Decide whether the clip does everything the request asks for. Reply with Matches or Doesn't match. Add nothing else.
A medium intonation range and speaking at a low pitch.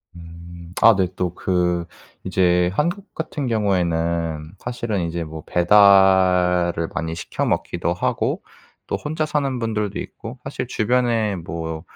Matches